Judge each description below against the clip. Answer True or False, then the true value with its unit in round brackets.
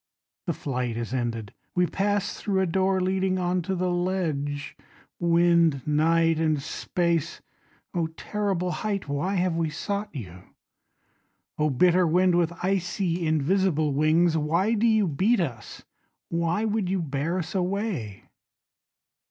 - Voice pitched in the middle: True (175 Hz)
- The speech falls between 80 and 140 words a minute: True (135 wpm)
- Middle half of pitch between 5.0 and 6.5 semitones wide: False (3.6 semitones)